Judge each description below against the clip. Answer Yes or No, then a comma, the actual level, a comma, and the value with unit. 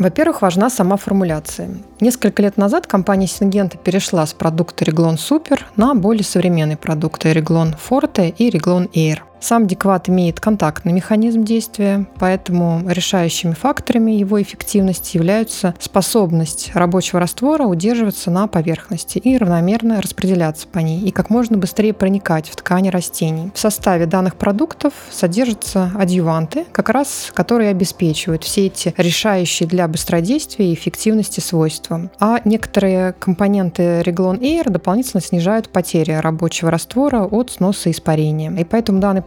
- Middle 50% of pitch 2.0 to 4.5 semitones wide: Yes, average, 3.8 semitones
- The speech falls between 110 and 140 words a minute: Yes, average, 135 wpm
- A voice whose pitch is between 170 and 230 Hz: Yes, high, 190 Hz